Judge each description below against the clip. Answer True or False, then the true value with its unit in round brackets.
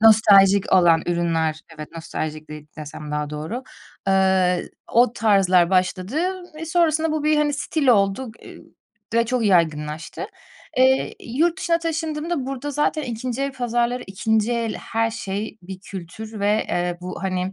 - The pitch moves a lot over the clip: True (6.5 semitones)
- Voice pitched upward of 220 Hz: False (210 Hz)